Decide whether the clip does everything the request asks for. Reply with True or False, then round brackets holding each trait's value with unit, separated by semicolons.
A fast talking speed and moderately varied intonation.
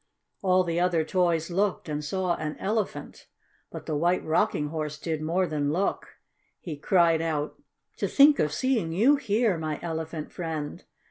False (160 wpm; 3.3 semitones)